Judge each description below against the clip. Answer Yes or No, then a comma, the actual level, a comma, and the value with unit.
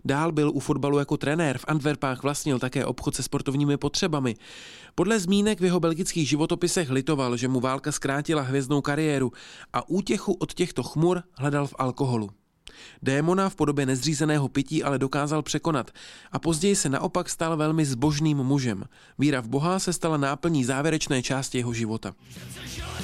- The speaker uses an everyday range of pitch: Yes, average, 3.2 semitones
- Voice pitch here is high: No, medium, 145 Hz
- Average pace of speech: Yes, average, 160 wpm